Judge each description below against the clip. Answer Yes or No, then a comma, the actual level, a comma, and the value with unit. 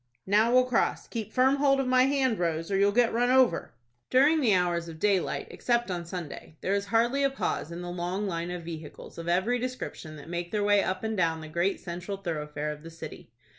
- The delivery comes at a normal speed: No, fast, 225 wpm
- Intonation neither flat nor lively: No, wide, 5.9 semitones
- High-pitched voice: Yes, high, 195 Hz